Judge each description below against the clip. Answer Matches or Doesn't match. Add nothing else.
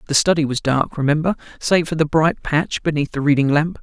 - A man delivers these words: Matches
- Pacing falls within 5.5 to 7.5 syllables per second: Matches